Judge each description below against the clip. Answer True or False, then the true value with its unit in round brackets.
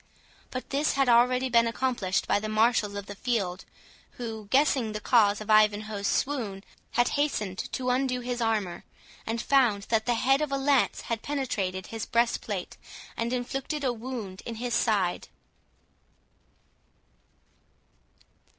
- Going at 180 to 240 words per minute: False (140 wpm)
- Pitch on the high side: True (230 Hz)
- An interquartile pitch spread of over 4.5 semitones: False (3.2 semitones)